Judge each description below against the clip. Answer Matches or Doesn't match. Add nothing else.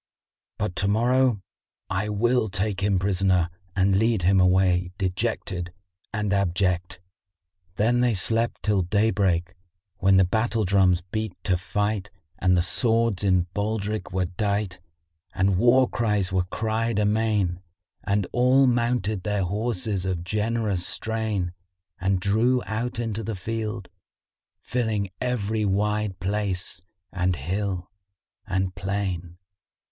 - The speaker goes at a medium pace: Doesn't match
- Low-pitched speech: Matches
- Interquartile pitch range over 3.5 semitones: Doesn't match